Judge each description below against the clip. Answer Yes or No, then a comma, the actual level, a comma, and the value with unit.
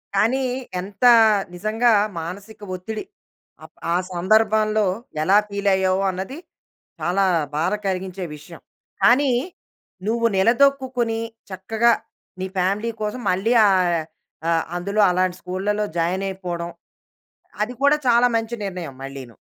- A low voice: No, high, 195 Hz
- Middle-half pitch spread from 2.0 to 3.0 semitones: No, average, 3.7 semitones